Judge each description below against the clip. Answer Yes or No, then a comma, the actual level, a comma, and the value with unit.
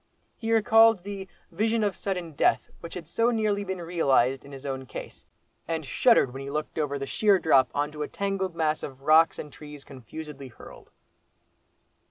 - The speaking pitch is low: No, medium, 160 Hz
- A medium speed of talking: Yes, average, 185 wpm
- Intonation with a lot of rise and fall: Yes, wide, 6.0 semitones